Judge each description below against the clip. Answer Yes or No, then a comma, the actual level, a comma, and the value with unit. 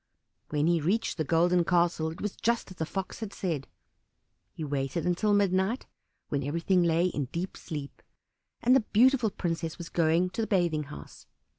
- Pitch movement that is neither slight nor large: Yes, average, 3.4 semitones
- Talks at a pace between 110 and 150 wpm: No, average, 175 wpm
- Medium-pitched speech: Yes, medium, 175 Hz